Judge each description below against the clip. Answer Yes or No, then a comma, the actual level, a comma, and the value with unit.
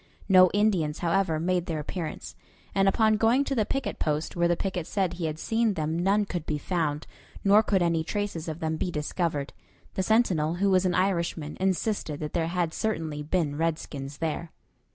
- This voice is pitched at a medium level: Yes, medium, 175 Hz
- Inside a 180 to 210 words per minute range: Yes, average, 190 wpm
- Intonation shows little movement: No, average, 3.8 semitones